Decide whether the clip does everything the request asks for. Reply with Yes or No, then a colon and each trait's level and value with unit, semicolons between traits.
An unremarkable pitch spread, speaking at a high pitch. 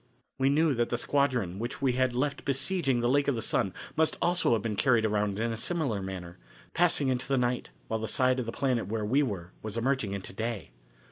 No: average, 4.2 semitones; low, 120 Hz